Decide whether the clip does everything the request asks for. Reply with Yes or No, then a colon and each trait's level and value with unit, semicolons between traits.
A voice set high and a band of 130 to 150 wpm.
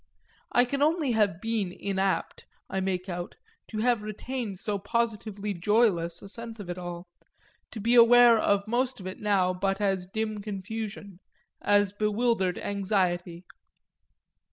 Yes: high, 205 Hz; average, 145 wpm